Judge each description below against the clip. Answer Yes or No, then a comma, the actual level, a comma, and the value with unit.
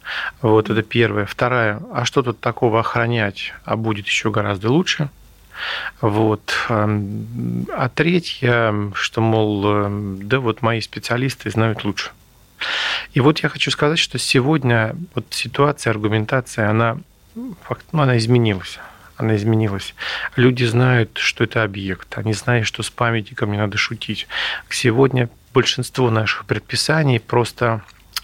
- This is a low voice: Yes, low, 115 Hz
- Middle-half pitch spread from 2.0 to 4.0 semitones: Yes, average, 2.9 semitones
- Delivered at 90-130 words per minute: Yes, average, 125 wpm